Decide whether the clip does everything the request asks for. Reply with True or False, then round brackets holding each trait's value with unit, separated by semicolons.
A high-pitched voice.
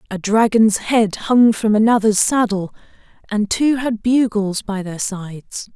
True (215 Hz)